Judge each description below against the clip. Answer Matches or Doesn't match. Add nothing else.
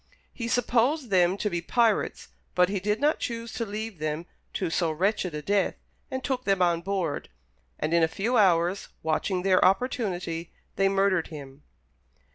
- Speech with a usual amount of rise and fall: Matches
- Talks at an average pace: Matches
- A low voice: Doesn't match